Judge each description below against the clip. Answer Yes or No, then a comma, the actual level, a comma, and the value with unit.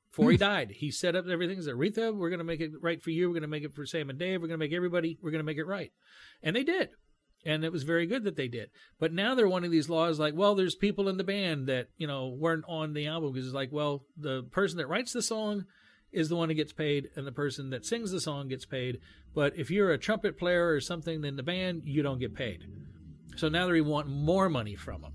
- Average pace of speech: No, fast, 280 wpm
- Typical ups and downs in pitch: Yes, average, 4.0 semitones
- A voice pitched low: No, medium, 160 Hz